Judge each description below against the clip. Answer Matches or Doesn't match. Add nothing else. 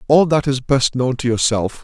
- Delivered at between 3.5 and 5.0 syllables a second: Matches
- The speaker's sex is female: Doesn't match